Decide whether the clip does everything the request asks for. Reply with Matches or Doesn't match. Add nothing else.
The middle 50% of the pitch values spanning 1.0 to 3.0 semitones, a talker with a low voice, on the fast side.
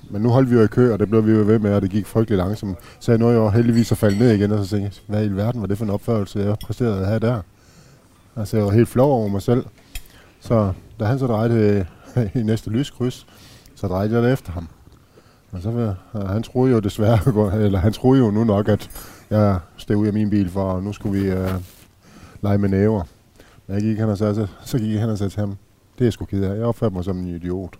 Matches